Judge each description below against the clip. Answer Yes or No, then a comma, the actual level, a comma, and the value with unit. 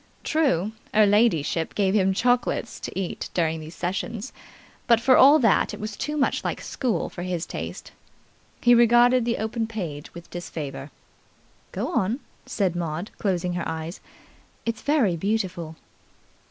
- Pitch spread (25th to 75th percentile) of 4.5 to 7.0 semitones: Yes, wide, 5.4 semitones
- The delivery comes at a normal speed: Yes, average, 150 wpm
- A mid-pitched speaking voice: No, high, 200 Hz